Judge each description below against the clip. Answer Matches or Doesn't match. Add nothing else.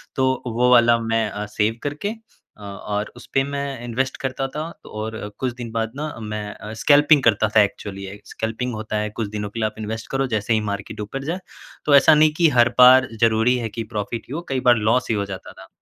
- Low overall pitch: Matches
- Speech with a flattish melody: Doesn't match